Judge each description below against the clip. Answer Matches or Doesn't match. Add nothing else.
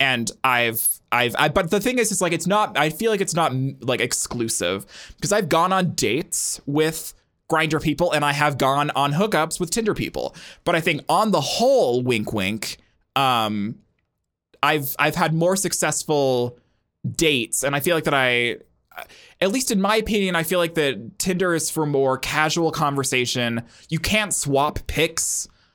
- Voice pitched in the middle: Matches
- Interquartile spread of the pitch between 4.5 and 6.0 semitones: Matches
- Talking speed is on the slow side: Doesn't match